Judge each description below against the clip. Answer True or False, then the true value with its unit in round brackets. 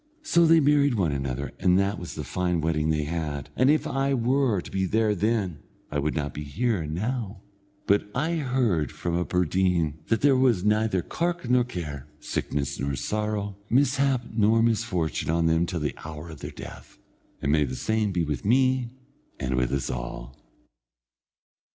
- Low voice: True (95 Hz)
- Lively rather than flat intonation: True (7.7 semitones)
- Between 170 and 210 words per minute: True (180 wpm)